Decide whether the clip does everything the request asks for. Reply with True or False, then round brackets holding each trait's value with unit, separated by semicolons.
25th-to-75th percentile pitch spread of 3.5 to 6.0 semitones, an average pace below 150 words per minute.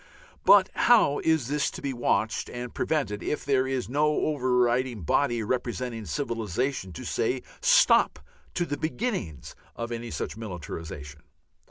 True (4.3 semitones; 140 wpm)